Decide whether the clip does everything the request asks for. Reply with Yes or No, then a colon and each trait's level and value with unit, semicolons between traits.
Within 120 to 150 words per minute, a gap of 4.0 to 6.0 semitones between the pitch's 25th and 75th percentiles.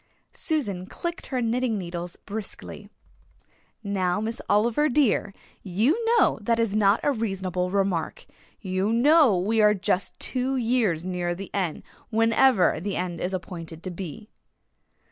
Yes: average, 140 wpm; average, 4.4 semitones